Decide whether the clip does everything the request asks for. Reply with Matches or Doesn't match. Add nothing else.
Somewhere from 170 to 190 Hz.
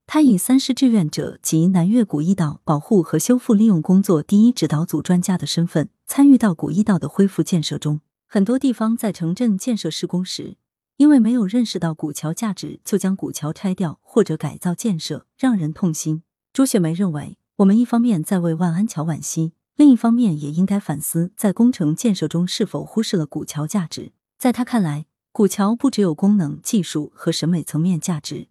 Matches